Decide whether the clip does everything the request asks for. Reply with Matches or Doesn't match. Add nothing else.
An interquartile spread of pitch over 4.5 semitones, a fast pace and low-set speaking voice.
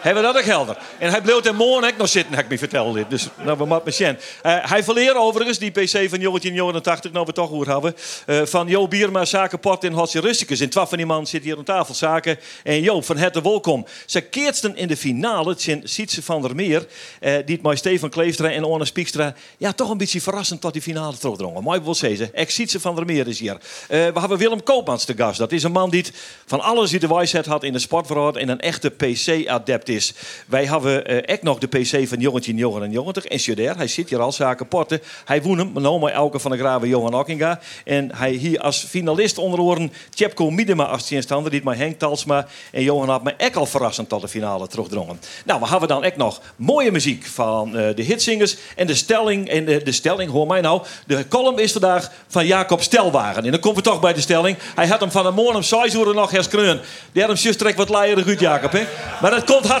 Doesn't match